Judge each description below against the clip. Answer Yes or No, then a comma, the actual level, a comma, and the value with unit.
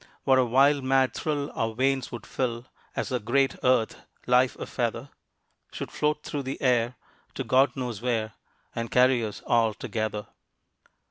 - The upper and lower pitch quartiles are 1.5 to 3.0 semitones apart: Yes, narrow, 2.5 semitones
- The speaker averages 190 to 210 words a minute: No, average, 160 wpm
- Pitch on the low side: Yes, low, 125 Hz